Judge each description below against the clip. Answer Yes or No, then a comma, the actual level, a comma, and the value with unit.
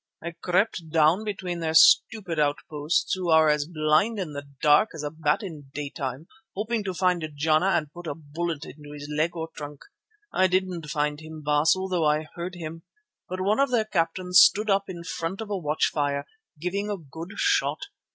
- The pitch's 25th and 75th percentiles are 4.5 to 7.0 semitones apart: No, average, 3.8 semitones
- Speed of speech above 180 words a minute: Yes, average, 190 wpm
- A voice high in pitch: No, medium, 165 Hz